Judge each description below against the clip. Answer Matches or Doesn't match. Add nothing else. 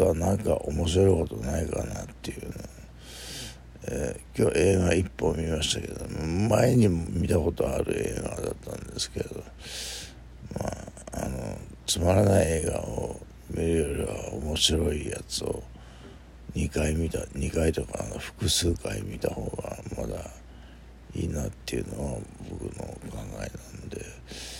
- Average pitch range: Matches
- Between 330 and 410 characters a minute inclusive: Doesn't match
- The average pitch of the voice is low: Matches